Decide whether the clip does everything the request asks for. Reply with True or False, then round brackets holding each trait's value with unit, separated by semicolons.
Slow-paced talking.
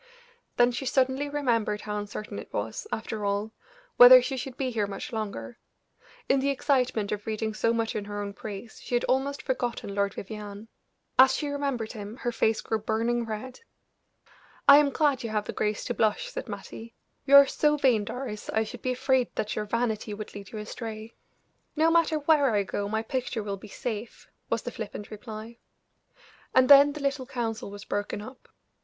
False (190 wpm)